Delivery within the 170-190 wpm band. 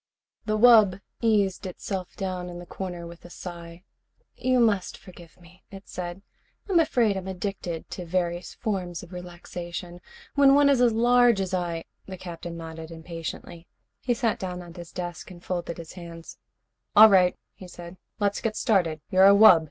Yes: average, 175 wpm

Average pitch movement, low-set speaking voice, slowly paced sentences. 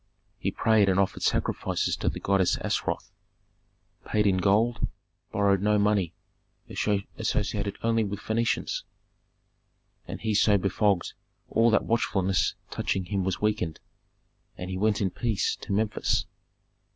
No: narrow, 2.0 semitones; low, 100 Hz; slow, 130 wpm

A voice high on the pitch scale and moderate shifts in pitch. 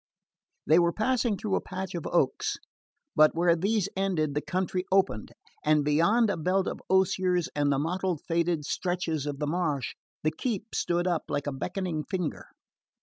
No: medium, 175 Hz; average, 3.7 semitones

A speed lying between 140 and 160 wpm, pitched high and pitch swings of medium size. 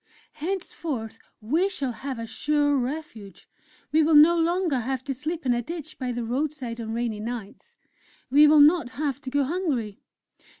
No: average, 170 wpm; very high, 280 Hz; average, 4.5 semitones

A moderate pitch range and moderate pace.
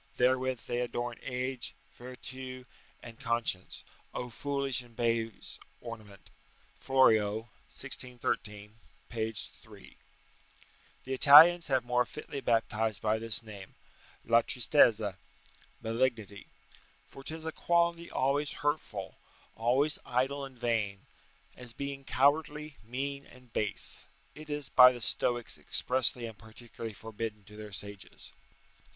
No: average, 3.5 semitones; slow, 120 wpm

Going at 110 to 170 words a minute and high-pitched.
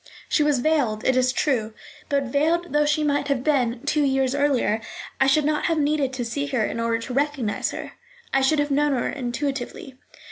No: fast, 205 wpm; very high, 275 Hz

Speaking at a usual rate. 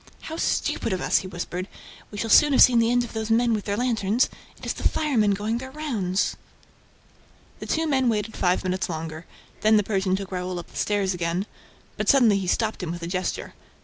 No: fast, 215 wpm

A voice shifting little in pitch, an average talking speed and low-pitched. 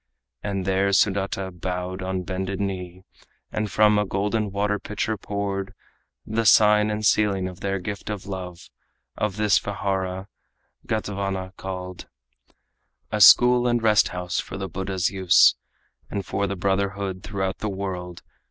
Yes: narrow, 1.7 semitones; average, 145 wpm; very low, 95 Hz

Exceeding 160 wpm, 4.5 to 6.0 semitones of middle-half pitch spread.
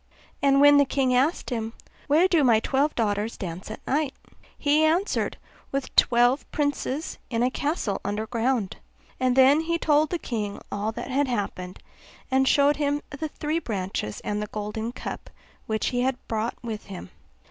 Yes: average, 170 wpm; average, 4.9 semitones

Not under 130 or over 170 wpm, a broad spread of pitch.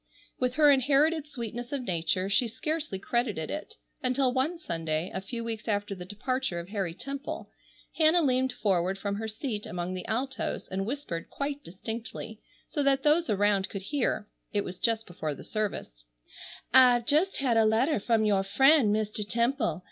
Yes: average, 165 wpm; wide, 5.7 semitones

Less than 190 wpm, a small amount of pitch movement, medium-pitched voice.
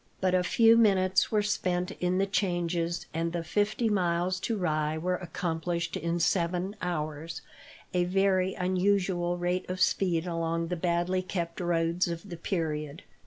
Yes: average, 155 wpm; narrow, 1.9 semitones; medium, 180 Hz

